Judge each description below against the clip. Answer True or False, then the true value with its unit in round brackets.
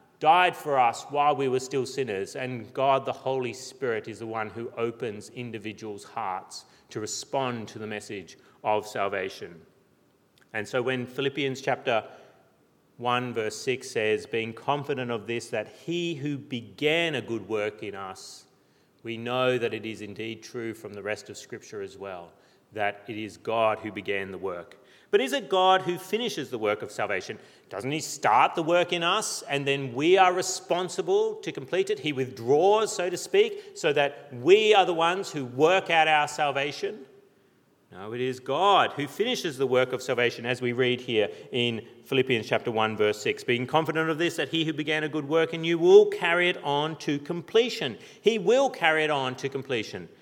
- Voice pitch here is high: False (140 Hz)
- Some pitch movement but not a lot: False (6.9 semitones)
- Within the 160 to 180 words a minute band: False (190 wpm)